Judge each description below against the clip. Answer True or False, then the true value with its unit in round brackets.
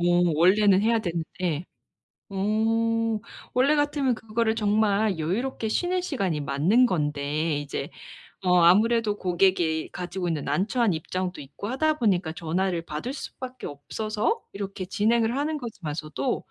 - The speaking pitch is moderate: False (195 Hz)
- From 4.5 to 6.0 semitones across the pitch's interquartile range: True (5.1 semitones)